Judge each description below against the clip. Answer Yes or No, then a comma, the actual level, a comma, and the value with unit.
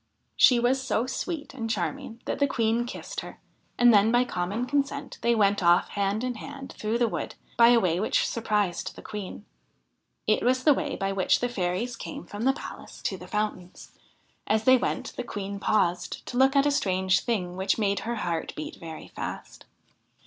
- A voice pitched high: Yes, high, 220 Hz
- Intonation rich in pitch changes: No, average, 4.2 semitones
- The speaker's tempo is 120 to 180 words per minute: No, average, 195 wpm